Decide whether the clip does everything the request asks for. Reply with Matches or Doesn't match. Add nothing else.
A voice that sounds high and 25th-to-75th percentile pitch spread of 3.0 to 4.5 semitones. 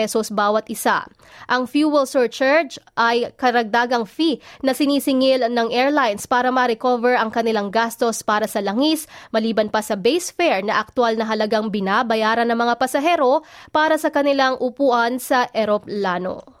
Matches